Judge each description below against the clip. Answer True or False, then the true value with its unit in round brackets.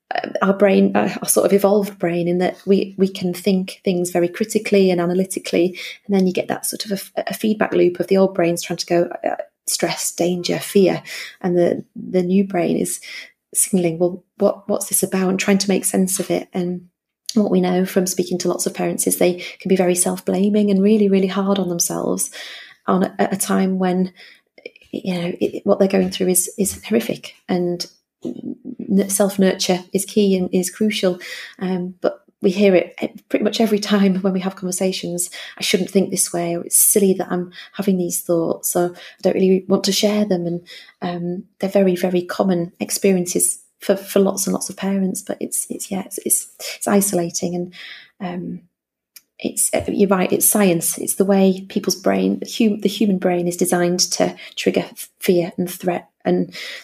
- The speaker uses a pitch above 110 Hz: True (190 Hz)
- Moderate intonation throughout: False (2.0 semitones)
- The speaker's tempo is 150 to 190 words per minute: False (200 wpm)